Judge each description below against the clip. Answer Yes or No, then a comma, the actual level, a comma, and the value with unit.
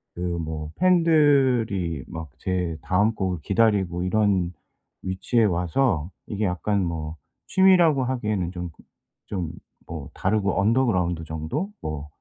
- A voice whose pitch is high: No, very low, 95 Hz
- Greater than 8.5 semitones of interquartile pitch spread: No, average, 5.3 semitones